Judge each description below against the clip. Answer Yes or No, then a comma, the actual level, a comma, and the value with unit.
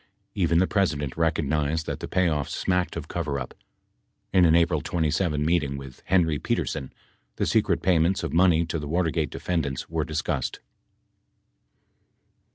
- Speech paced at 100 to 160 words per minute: Yes, average, 155 wpm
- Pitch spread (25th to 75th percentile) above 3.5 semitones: No, average, 2.8 semitones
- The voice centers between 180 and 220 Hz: No, very low, 80 Hz